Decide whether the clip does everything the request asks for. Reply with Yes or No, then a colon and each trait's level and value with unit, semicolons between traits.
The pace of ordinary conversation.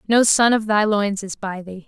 No: fast, 255 wpm